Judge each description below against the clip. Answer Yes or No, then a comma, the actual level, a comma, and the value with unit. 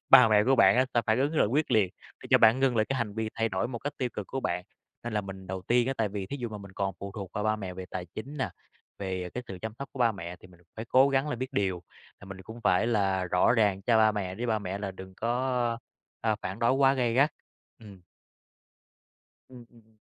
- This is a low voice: Yes, low, 110 Hz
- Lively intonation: No, average, 4.2 semitones